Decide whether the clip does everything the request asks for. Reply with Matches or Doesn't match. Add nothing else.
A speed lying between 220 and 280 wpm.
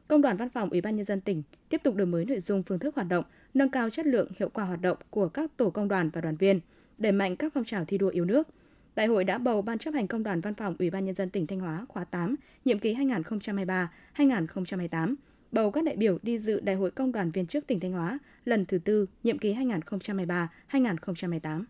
Matches